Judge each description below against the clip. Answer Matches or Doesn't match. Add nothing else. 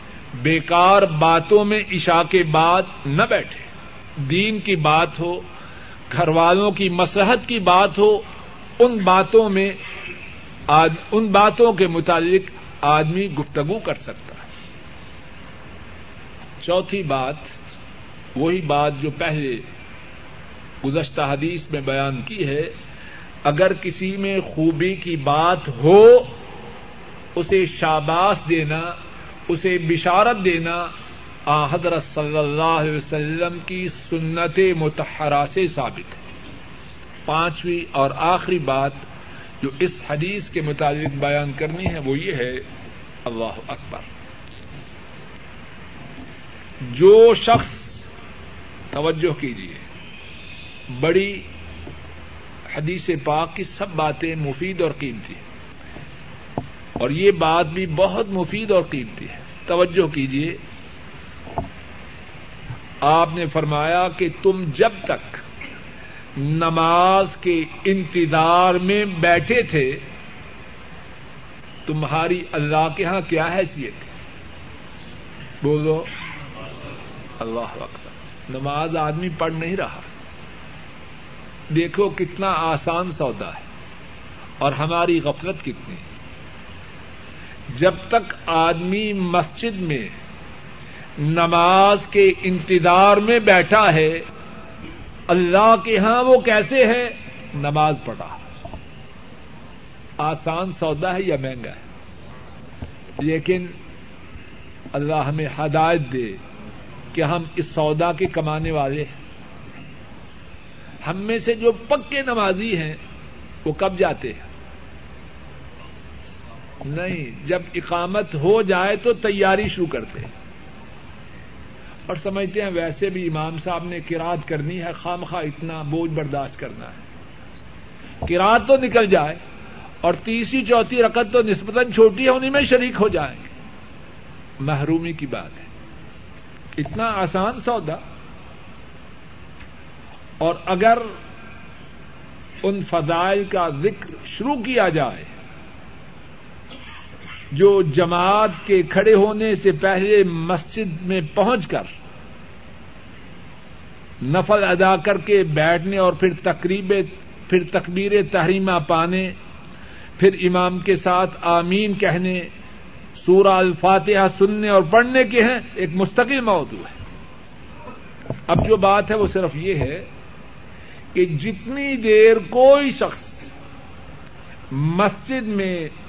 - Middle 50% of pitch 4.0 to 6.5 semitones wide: Matches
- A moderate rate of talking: Doesn't match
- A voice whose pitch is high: Doesn't match